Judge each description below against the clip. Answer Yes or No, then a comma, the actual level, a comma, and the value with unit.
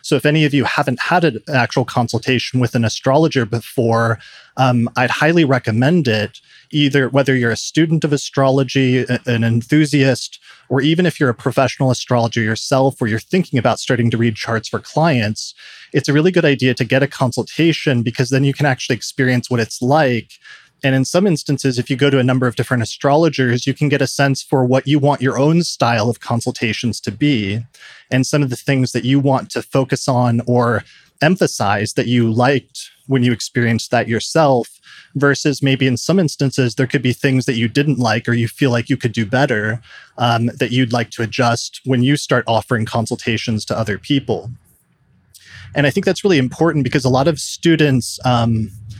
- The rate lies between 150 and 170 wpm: No, average, 195 wpm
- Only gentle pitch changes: No, average, 3.2 semitones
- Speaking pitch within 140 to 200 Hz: No, low, 130 Hz